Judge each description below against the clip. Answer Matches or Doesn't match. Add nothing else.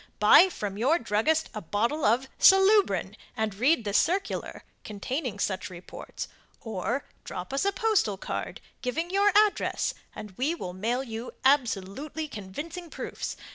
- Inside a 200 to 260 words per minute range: Doesn't match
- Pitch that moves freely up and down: Matches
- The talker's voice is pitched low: Doesn't match